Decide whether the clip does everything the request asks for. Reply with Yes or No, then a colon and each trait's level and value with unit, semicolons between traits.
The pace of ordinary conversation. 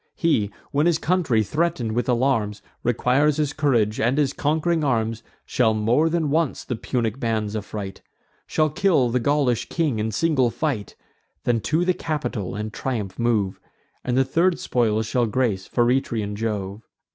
Yes: average, 155 wpm